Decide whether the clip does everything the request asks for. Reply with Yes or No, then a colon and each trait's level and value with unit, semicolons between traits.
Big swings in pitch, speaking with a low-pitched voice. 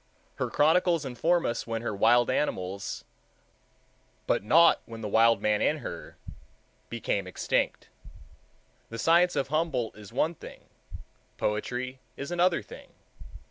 Yes: wide, 6.6 semitones; low, 125 Hz